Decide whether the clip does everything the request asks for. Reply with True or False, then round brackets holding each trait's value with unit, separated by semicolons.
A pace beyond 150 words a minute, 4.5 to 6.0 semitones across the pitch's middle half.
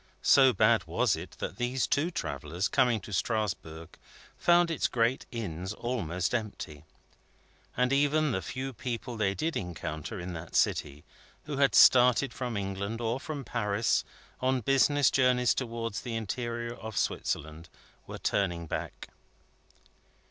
False (140 wpm; 5.2 semitones)